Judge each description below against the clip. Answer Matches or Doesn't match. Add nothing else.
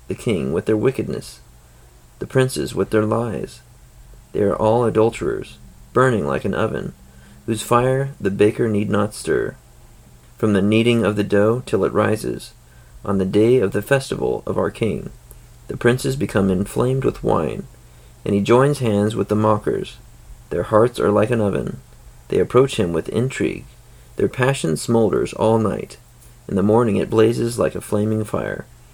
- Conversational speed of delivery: Matches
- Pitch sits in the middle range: Doesn't match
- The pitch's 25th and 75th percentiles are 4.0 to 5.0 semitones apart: Doesn't match